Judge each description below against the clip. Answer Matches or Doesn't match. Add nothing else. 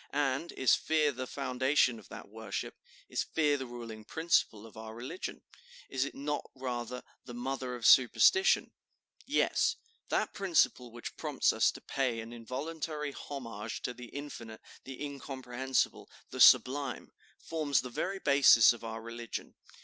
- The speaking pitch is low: Matches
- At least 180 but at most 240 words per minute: Doesn't match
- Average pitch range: Matches